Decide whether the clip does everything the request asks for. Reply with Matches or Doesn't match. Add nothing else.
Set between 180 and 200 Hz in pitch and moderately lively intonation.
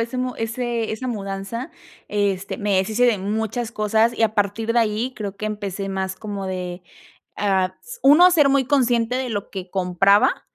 Doesn't match